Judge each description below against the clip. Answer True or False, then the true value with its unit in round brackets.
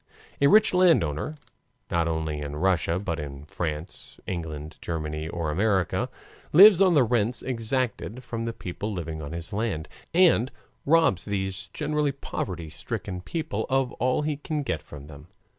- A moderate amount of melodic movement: False (8.8 semitones)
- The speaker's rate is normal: True (155 wpm)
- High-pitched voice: False (95 Hz)